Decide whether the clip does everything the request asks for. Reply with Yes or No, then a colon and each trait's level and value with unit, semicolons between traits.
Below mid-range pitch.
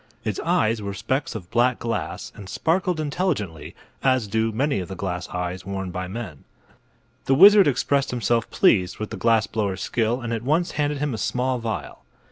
Yes: low, 115 Hz